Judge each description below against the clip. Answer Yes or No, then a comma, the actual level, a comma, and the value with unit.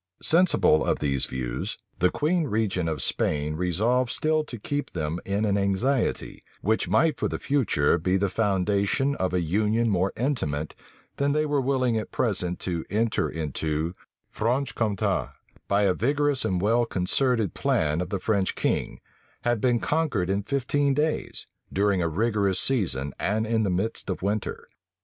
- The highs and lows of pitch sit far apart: Yes, wide, 5.9 semitones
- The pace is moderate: Yes, average, 165 wpm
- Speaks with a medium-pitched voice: No, low, 105 Hz